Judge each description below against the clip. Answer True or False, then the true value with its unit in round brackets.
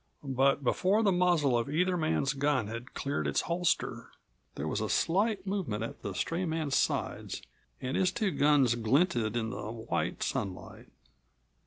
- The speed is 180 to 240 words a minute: False (160 wpm)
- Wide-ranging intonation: True (7.3 semitones)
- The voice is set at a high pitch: False (145 Hz)